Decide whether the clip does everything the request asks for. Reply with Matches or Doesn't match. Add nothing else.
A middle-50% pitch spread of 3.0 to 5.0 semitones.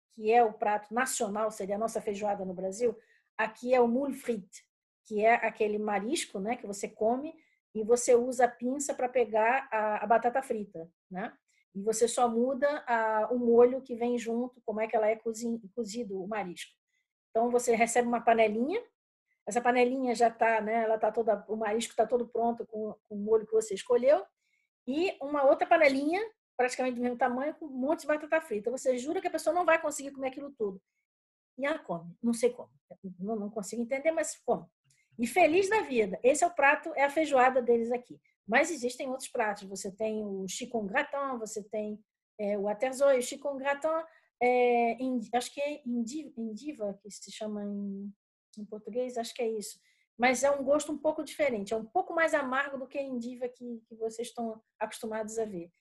Matches